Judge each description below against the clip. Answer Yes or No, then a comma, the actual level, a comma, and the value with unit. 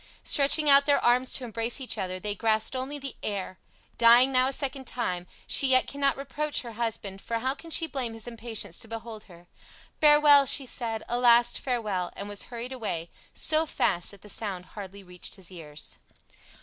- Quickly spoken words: No, average, 190 wpm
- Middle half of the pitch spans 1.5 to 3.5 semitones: No, average, 4.7 semitones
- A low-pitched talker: No, high, 235 Hz